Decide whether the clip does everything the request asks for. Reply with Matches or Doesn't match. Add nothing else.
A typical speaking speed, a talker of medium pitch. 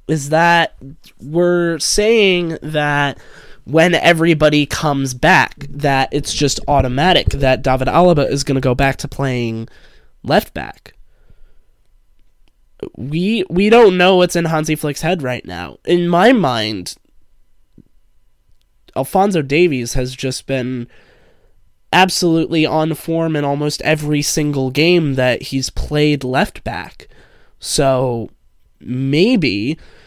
Doesn't match